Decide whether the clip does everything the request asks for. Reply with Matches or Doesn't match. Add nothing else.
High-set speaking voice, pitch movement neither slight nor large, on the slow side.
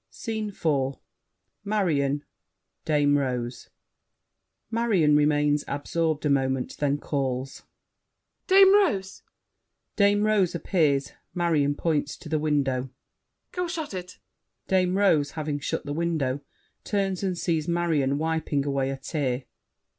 Doesn't match